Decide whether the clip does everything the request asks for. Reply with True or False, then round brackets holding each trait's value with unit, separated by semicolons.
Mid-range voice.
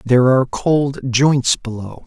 False (130 Hz)